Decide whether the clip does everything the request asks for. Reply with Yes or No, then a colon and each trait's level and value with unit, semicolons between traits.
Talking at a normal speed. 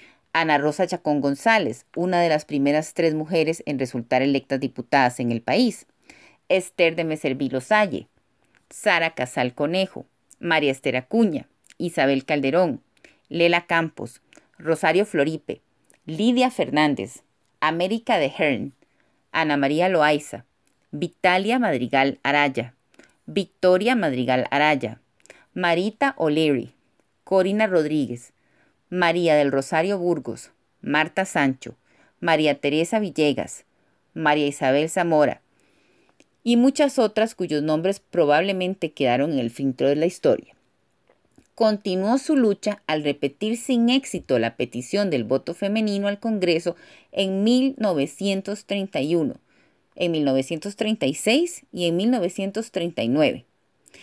No: slow, 105 wpm